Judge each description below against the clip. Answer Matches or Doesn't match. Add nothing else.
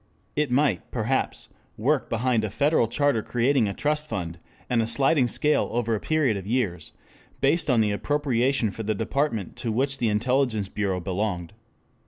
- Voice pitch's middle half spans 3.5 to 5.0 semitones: Matches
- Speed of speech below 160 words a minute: Doesn't match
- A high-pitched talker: Doesn't match